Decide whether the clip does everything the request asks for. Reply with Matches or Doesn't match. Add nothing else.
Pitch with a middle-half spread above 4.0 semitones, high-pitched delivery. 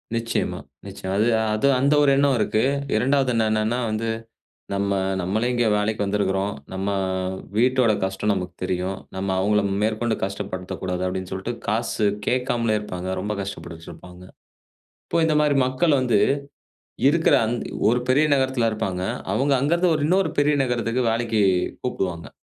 Doesn't match